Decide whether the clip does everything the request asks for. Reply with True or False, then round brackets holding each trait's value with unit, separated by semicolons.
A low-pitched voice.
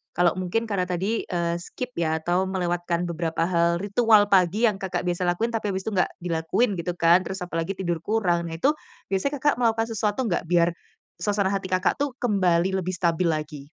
False (185 Hz)